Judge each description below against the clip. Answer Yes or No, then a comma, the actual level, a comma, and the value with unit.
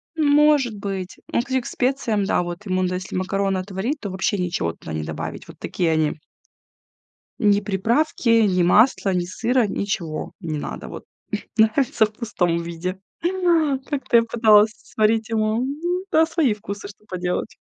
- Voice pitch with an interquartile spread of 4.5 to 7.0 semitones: Yes, average, 5.2 semitones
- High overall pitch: Yes, high, 210 Hz